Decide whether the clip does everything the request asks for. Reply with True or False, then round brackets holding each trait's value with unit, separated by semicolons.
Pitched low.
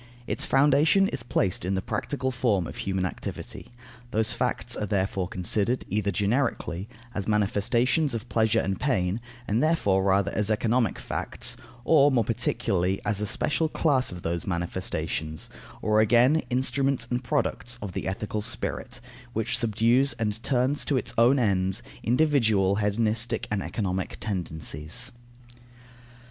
True (110 Hz)